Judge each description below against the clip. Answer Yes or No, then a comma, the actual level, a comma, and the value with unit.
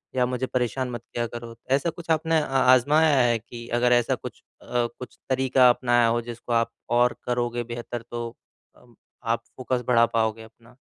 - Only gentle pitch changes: Yes, narrow, 1.5 semitones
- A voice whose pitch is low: Yes, low, 120 Hz